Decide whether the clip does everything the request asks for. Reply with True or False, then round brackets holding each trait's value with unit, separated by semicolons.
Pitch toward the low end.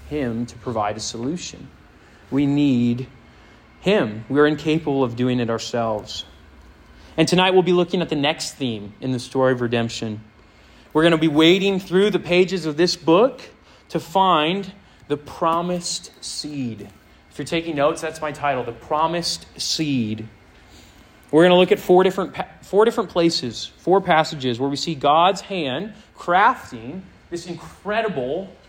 False (150 Hz)